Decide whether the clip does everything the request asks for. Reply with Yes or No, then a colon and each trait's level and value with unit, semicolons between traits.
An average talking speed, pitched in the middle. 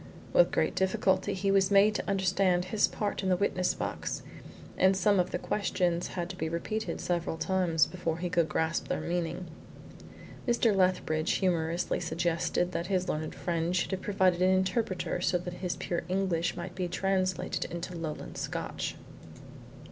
Yes: average, 165 wpm; medium, 180 Hz